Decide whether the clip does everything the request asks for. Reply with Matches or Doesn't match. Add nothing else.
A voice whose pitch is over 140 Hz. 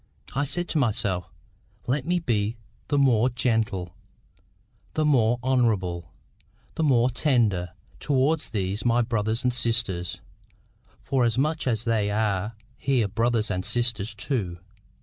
Doesn't match